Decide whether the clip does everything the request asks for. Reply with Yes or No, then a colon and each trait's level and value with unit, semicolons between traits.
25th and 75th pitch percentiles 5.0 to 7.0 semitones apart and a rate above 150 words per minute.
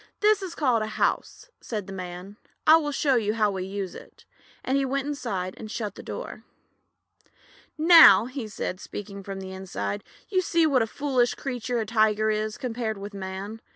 Yes: wide, 5.4 semitones; average, 185 wpm